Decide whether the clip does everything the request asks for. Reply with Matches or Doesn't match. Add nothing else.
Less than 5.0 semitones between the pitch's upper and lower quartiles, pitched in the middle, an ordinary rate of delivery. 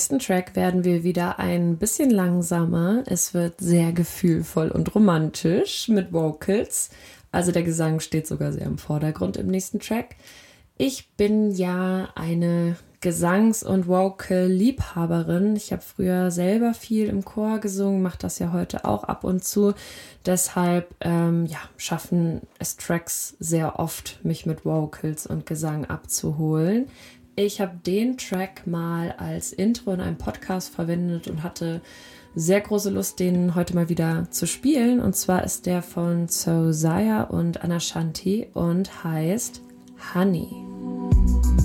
Matches